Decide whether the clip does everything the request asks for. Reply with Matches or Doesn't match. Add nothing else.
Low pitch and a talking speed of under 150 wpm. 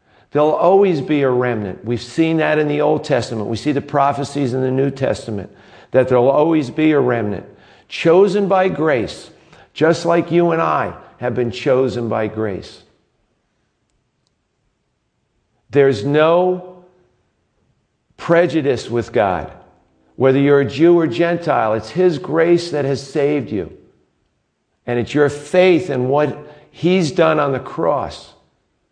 Doesn't match